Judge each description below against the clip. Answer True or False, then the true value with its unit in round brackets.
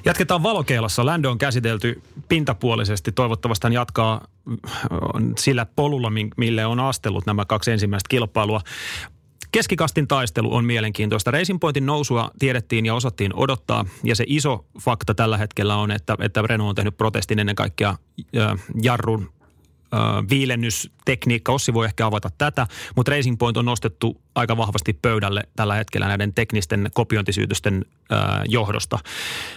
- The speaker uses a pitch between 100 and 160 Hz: True (115 Hz)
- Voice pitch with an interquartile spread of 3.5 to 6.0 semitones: False (2.8 semitones)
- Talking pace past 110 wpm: True (130 wpm)